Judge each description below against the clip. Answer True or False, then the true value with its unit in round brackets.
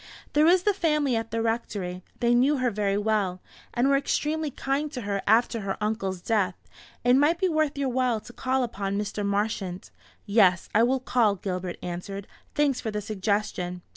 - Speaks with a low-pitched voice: False (225 Hz)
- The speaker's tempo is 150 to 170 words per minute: False (185 wpm)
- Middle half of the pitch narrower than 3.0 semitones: False (5.1 semitones)